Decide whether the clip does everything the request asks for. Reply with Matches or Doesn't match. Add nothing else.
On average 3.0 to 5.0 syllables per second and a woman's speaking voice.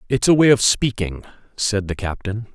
Doesn't match